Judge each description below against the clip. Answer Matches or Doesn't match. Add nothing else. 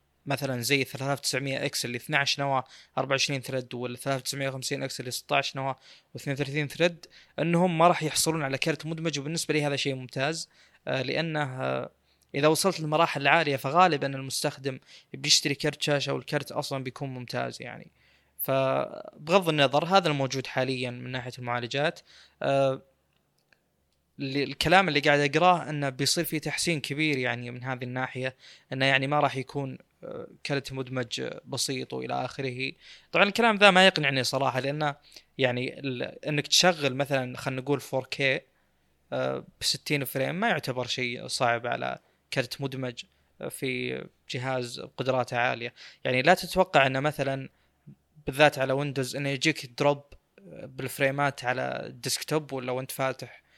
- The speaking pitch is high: Doesn't match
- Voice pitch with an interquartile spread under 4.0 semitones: Matches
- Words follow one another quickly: Matches